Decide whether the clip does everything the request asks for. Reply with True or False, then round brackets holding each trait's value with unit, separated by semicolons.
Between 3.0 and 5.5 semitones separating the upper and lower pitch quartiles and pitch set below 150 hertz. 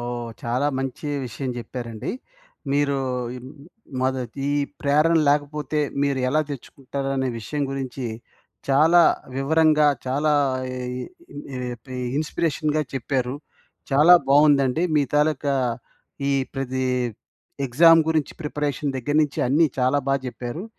False (2.6 semitones; 140 Hz)